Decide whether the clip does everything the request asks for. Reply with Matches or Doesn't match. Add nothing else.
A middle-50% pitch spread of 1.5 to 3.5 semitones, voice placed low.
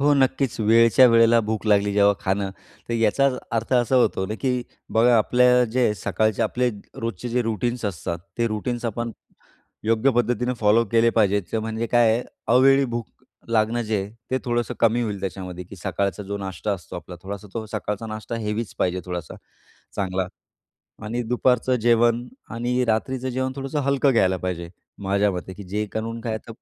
Matches